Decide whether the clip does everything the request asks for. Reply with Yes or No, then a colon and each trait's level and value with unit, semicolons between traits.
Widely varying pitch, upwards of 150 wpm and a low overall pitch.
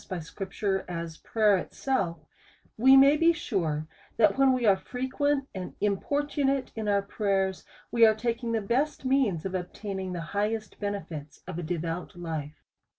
No: wide, 6.0 semitones; average, 170 wpm; high, 205 Hz